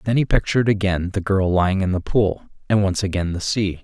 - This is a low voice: Yes, very low, 95 Hz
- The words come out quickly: Yes, fast, 235 wpm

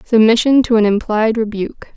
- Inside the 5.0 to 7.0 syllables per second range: Yes, 5.6 syllables/s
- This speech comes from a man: No, female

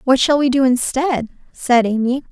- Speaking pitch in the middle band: No, very high, 260 Hz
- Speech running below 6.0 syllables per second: Yes, 4.7 syllables/s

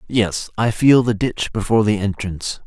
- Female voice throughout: No, male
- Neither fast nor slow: Yes, average, 180 wpm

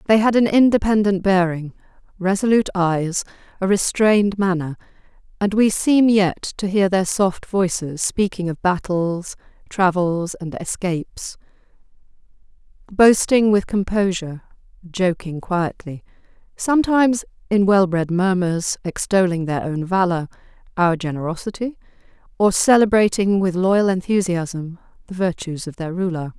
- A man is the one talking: No, female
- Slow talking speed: Yes, slow, 115 wpm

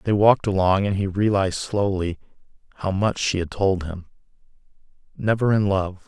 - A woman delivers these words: No, male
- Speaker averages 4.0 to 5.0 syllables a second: No, 5.2 syllables/s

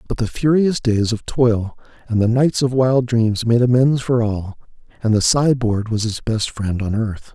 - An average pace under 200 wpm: No, fast, 205 wpm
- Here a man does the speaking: Yes, male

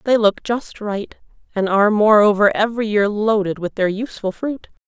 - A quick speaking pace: No, average, 170 wpm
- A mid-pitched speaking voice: No, high, 210 Hz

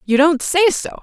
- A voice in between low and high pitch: No, very high, 315 Hz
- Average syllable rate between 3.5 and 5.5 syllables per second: Yes, 4.4 syllables/s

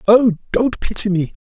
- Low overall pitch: No, high, 210 Hz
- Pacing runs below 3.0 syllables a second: No, 4.6 syllables/s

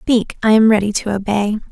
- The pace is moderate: No, fast, 210 wpm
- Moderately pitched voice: No, high, 210 Hz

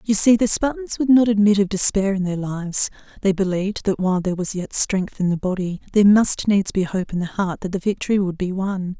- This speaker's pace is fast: Yes, fast, 245 wpm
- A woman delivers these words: Yes, female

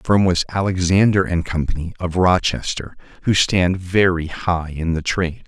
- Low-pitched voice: Yes, very low, 90 Hz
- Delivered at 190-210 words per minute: No, average, 165 wpm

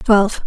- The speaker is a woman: Yes, female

